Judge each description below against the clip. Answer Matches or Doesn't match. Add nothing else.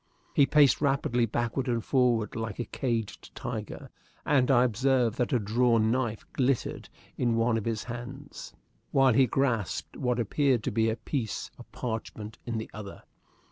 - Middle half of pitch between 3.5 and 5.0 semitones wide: Doesn't match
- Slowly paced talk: Doesn't match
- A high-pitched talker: Doesn't match